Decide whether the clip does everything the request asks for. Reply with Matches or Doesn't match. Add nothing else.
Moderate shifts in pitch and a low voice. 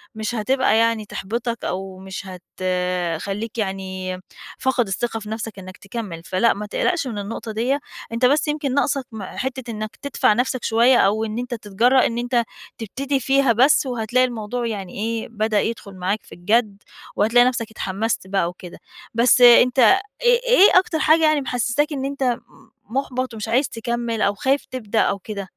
Doesn't match